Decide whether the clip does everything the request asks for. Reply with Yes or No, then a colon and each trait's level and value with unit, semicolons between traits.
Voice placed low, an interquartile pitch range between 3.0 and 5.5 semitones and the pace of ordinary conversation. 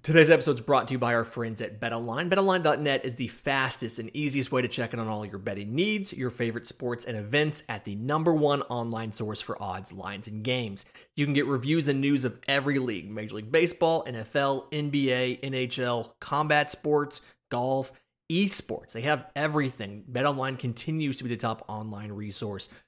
Yes: low, 130 Hz; average, 4.3 semitones; average, 190 wpm